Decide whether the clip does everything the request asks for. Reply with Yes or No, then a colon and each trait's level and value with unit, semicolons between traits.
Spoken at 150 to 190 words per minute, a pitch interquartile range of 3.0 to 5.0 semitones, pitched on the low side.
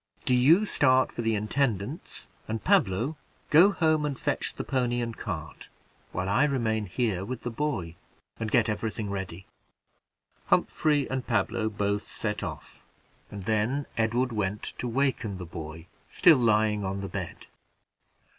Yes: average, 155 wpm; average, 4.6 semitones; low, 110 Hz